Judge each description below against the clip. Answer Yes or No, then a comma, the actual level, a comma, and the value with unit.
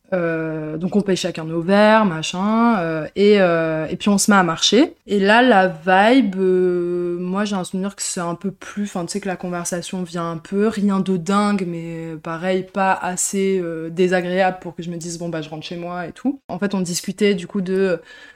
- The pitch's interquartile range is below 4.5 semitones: Yes, average, 2.7 semitones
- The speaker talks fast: Yes, fast, 230 wpm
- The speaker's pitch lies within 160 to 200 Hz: Yes, medium, 185 Hz